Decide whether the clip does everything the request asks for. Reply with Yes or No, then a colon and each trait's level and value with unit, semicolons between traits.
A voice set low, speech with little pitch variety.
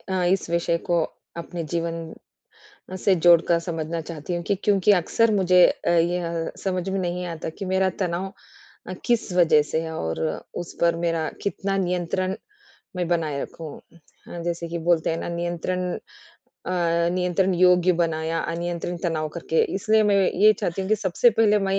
No: medium, 175 Hz; narrow, 2.1 semitones